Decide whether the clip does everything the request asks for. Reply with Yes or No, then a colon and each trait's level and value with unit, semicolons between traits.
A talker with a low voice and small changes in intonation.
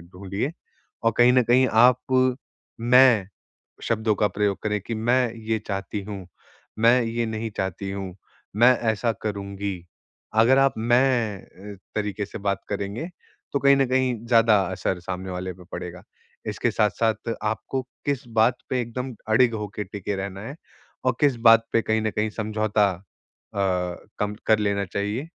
No: low, 110 Hz; average, 3.4 semitones